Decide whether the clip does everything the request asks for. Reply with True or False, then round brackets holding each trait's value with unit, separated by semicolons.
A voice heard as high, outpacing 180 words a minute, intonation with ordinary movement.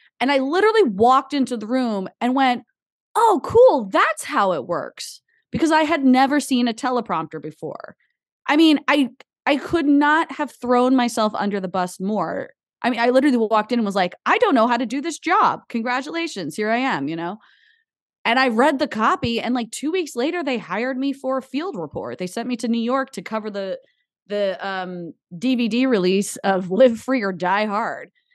True (250 Hz; 200 wpm; 4.9 semitones)